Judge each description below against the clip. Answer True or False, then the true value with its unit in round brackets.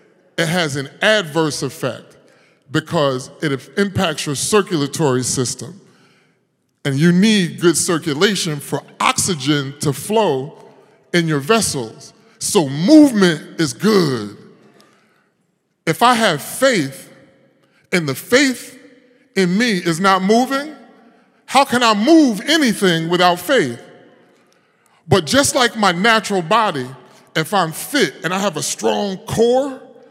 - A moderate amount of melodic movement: False (7.0 semitones)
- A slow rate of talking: True (120 wpm)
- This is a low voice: False (180 Hz)